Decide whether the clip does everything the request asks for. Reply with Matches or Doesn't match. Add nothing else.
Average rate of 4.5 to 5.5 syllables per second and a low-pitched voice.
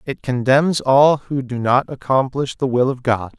Doesn't match